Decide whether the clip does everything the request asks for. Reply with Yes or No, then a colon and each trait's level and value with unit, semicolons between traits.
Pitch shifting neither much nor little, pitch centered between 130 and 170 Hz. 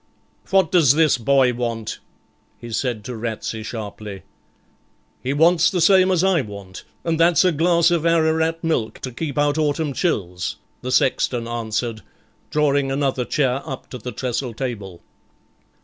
No: wide, 5.7 semitones; low, 135 Hz